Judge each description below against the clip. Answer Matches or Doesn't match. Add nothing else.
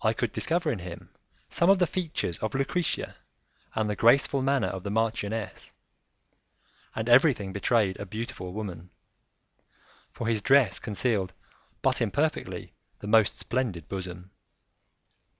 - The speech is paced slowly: Matches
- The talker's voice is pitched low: Matches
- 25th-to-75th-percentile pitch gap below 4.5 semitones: Doesn't match